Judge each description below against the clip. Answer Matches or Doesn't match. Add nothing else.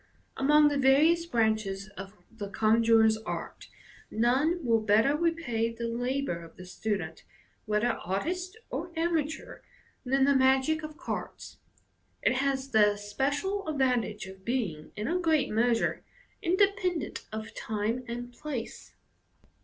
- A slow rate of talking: Matches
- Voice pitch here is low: Doesn't match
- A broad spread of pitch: Matches